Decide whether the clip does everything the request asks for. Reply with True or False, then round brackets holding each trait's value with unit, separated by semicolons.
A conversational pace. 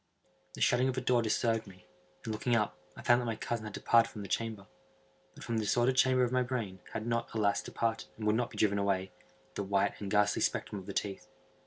False (235 wpm)